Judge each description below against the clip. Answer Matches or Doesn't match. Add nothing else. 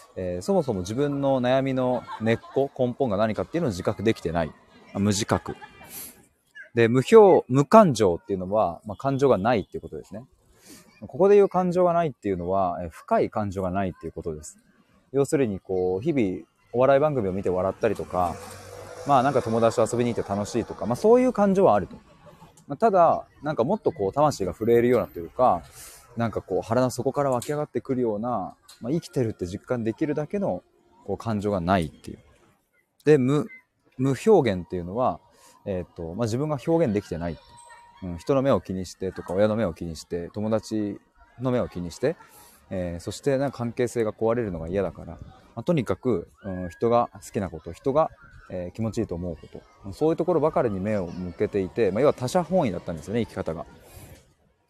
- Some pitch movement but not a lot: Doesn't match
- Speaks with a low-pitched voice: Matches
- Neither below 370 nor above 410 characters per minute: Matches